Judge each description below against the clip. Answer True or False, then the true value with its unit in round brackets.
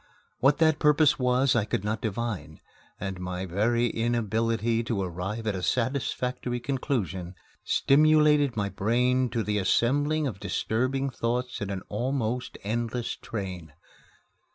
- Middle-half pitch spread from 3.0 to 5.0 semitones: True (4.1 semitones)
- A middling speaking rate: False (130 wpm)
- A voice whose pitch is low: True (115 Hz)